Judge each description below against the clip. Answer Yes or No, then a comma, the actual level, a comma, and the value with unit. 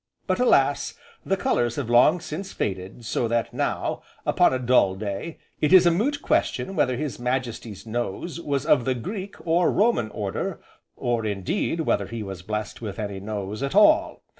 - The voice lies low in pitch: Yes, low, 125 Hz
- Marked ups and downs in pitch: Yes, wide, 7.8 semitones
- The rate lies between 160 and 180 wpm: Yes, average, 175 wpm